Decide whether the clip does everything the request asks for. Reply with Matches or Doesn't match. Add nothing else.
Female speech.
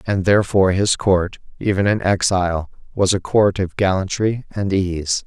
Doesn't match